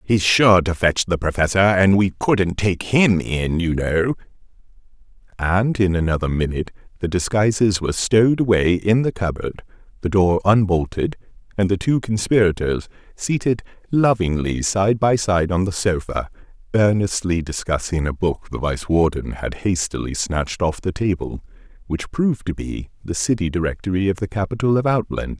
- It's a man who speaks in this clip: Yes, male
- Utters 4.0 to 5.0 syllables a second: Yes, 4.9 syllables/s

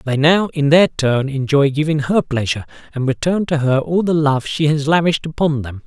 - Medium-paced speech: No, fast, 215 wpm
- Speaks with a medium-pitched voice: Yes, medium, 150 Hz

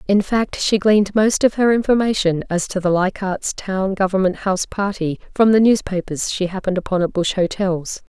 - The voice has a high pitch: Yes, high, 195 Hz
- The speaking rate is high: No, average, 185 wpm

